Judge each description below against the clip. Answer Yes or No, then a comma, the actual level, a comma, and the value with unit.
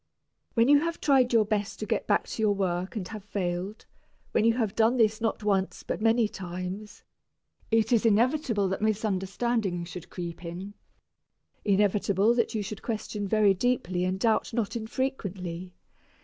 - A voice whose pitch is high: Yes, high, 210 Hz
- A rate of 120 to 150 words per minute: No, average, 165 wpm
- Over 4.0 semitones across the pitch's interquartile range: No, average, 3.2 semitones